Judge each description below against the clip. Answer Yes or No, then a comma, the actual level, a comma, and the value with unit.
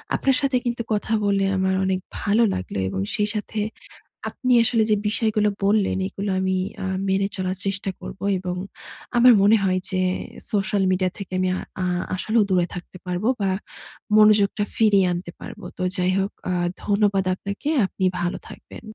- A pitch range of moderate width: No, narrow, 2.3 semitones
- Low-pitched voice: No, high, 195 Hz